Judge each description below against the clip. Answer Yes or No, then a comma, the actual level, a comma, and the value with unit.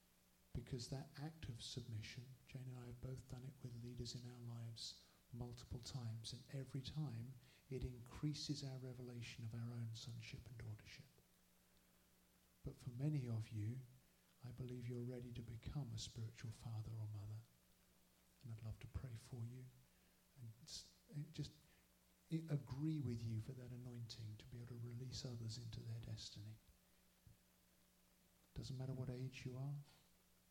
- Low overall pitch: Yes, low, 120 Hz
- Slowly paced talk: No, average, 155 wpm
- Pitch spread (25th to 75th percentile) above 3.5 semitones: No, average, 2.9 semitones